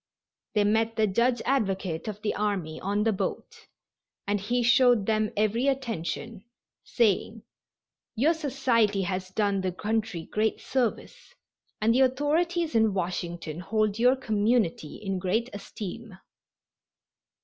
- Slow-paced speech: Yes, slow, 125 wpm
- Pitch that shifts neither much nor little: Yes, average, 3.6 semitones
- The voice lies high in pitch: Yes, high, 215 Hz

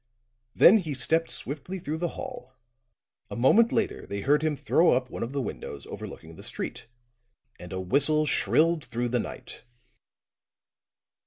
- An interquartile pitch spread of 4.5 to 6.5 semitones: Yes, average, 5.1 semitones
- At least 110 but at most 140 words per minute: No, average, 155 wpm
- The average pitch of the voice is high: No, medium, 140 Hz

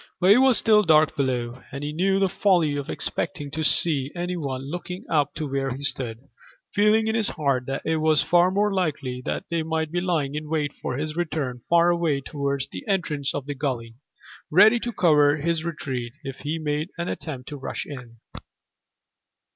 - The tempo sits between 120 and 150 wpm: No, average, 195 wpm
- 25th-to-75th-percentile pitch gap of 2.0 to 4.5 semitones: Yes, average, 4.1 semitones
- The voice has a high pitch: No, medium, 155 Hz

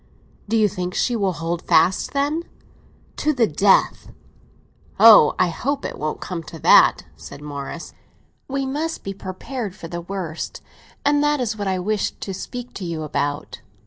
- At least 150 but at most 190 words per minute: Yes, average, 170 wpm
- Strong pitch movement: Yes, wide, 6.6 semitones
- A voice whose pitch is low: No, high, 195 Hz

